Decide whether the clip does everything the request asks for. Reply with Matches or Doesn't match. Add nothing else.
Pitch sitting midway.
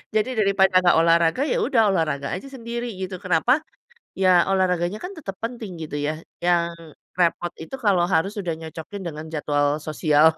Matches